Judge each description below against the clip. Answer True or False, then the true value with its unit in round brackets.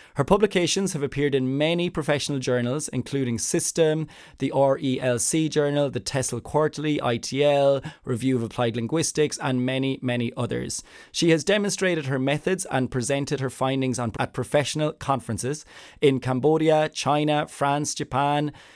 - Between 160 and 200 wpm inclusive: False (140 wpm)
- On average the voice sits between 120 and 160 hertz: True (140 Hz)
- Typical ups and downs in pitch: True (3.0 semitones)